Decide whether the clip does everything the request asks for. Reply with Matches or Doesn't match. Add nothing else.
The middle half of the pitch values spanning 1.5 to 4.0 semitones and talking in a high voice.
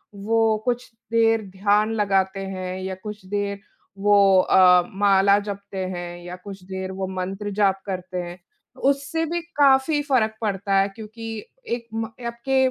Matches